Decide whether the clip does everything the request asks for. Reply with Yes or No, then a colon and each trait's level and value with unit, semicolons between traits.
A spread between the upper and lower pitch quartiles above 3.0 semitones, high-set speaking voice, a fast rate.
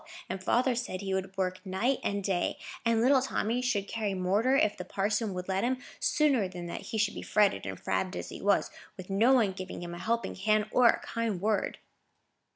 Yes: average, 3.6 semitones; high, 205 Hz; fast, 215 wpm